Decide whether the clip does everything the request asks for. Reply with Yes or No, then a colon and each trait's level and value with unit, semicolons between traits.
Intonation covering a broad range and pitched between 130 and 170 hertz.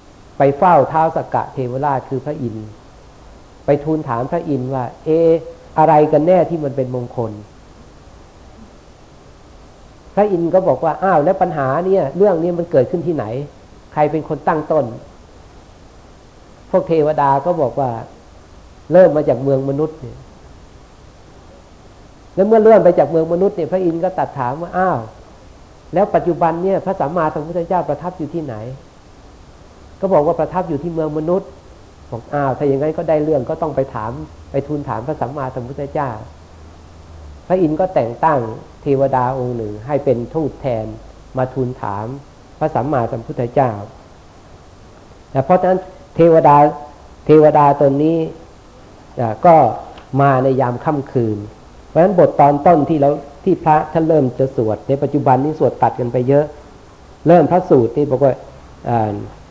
Yes: wide, 6.1 semitones; medium, 140 Hz